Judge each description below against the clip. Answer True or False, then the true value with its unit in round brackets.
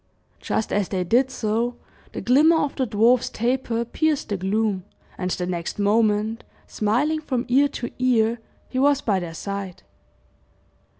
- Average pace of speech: True (155 wpm)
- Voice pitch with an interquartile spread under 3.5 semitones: False (4.1 semitones)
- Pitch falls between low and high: False (230 Hz)